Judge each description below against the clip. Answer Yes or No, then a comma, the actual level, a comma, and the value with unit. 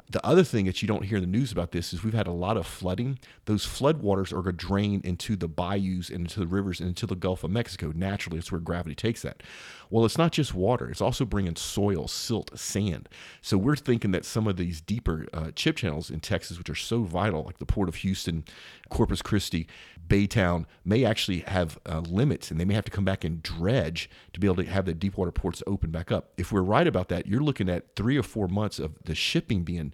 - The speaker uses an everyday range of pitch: Yes, average, 3.6 semitones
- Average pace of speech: No, fast, 245 wpm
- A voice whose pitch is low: Yes, very low, 95 Hz